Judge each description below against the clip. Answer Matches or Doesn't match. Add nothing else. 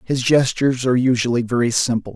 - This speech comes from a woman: Doesn't match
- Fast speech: Doesn't match